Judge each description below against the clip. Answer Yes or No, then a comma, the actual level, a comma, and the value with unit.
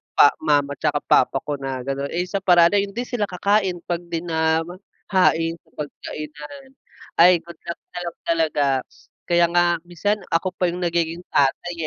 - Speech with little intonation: Yes, narrow, 2.2 semitones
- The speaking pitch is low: No, medium, 170 Hz